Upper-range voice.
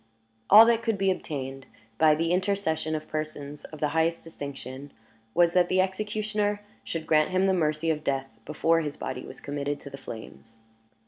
No: medium, 160 Hz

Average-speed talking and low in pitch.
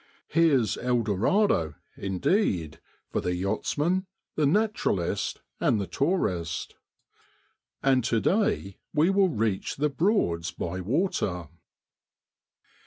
No: slow, 105 wpm; low, 120 Hz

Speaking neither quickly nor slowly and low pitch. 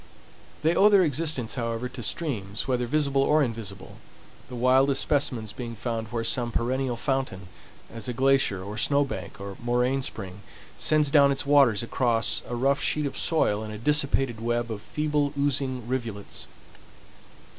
Yes: average, 155 wpm; low, 125 Hz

